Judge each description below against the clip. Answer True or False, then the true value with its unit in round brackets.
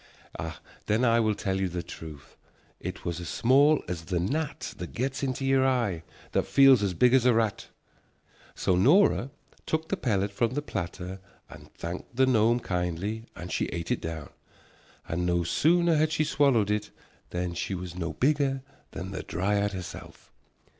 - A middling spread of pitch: False (6.9 semitones)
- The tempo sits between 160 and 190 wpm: True (175 wpm)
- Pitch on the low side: True (105 Hz)